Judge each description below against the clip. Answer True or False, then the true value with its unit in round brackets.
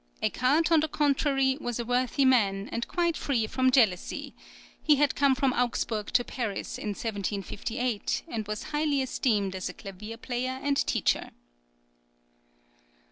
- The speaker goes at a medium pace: True (145 wpm)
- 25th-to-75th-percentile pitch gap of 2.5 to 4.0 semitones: False (4.6 semitones)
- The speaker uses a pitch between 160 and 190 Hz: False (245 Hz)